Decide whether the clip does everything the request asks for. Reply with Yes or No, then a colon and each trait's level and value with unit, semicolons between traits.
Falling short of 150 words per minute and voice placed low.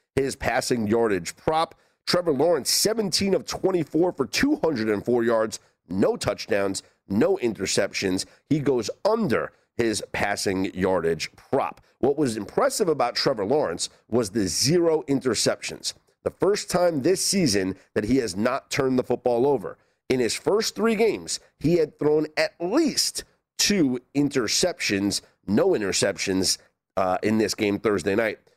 Yes: average, 140 wpm; low, 130 Hz